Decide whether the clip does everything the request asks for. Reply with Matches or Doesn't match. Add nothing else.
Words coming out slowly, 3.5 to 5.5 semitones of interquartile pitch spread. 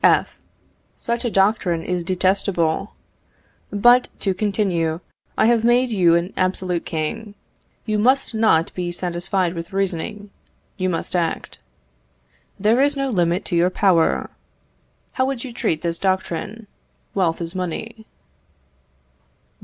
Matches